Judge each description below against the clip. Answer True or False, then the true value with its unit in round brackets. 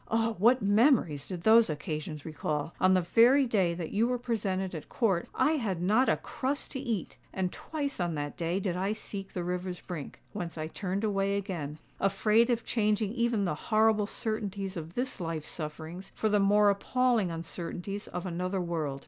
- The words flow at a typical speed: True (180 wpm)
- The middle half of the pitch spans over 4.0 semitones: True (4.5 semitones)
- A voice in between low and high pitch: False (195 Hz)